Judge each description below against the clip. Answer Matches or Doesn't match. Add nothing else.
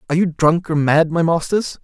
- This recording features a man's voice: Matches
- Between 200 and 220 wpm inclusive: Doesn't match